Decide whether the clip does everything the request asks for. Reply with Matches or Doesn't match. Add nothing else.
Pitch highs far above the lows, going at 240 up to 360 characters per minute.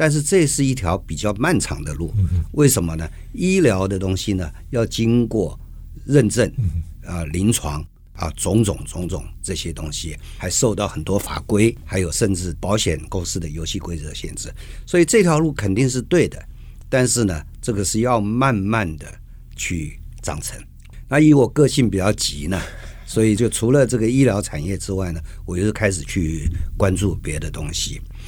Matches